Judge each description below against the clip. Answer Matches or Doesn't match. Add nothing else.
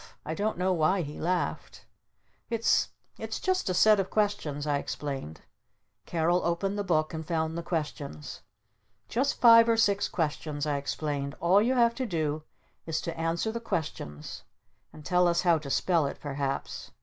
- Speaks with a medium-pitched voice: Matches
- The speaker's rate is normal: Matches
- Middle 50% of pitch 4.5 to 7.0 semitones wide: Matches